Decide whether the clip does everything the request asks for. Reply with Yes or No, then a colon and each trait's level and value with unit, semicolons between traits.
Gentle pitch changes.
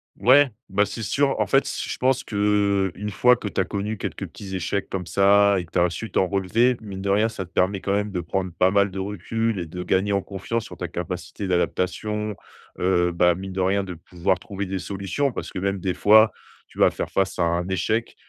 Yes: narrow, 2.3 semitones